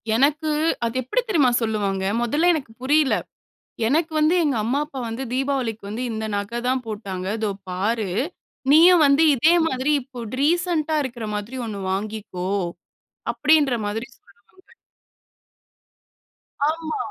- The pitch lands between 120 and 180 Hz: No, very high, 255 Hz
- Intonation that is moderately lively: No, wide, 5.9 semitones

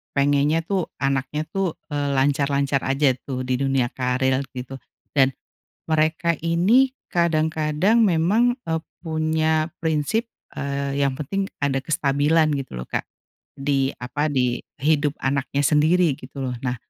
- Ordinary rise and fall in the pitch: Yes, average, 3.0 semitones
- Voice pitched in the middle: Yes, medium, 145 Hz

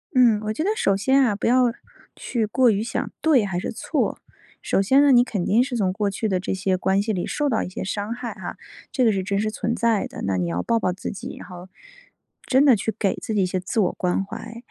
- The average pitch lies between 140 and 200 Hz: No, high, 215 Hz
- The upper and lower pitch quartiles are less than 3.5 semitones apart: No, average, 4.0 semitones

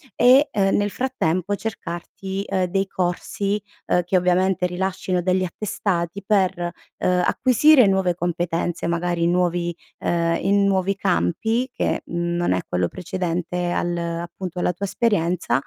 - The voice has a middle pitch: Yes, medium, 180 Hz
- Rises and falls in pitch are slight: Yes, narrow, 2.3 semitones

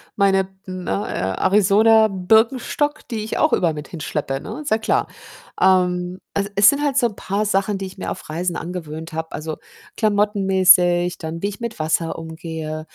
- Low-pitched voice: No, high, 190 Hz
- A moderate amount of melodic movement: Yes, average, 4.2 semitones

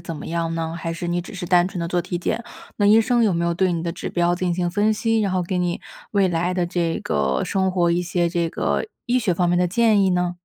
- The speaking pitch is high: No, medium, 175 Hz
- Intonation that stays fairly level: Yes, narrow, 1.9 semitones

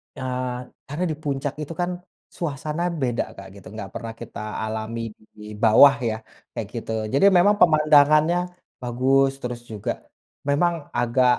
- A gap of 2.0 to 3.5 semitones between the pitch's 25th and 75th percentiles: No, average, 4.4 semitones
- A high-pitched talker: No, low, 135 Hz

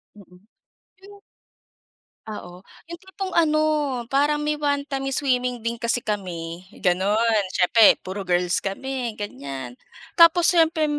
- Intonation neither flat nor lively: No, wide, 8.2 semitones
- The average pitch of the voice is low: No, high, 235 Hz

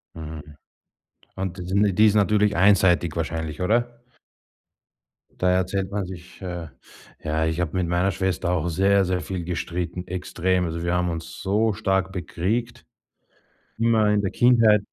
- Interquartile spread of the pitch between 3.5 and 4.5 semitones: No, average, 2.7 semitones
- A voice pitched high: No, very low, 90 Hz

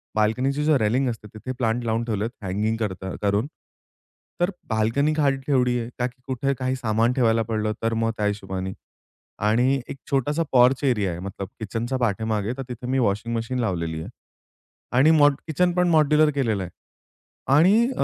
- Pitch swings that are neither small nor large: Yes, average, 4.1 semitones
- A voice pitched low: Yes, low, 120 Hz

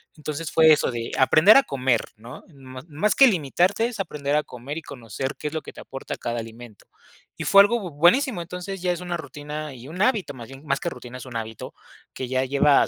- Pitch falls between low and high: Yes, medium, 150 Hz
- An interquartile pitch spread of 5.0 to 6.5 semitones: Yes, average, 5.3 semitones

